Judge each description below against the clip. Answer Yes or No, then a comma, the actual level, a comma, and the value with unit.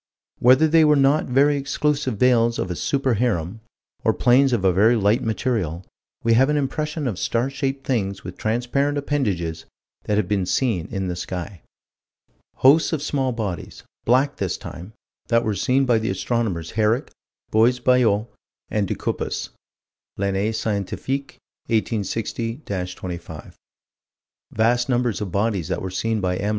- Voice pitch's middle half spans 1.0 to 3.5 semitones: No, average, 5.2 semitones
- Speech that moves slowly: No, average, 155 wpm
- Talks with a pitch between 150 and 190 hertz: No, low, 115 Hz